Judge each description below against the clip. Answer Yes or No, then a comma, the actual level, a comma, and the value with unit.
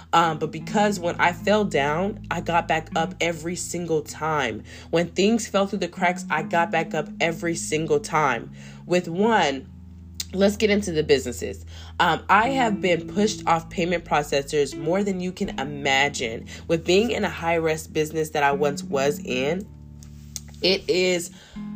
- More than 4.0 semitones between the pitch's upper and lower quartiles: Yes, average, 4.5 semitones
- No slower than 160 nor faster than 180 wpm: Yes, average, 165 wpm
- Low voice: No, medium, 165 Hz